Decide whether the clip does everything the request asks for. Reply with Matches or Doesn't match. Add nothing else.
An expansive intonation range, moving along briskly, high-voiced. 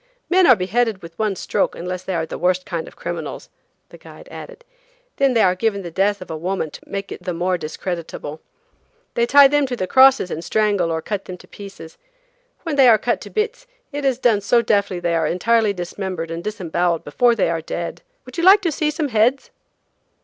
Matches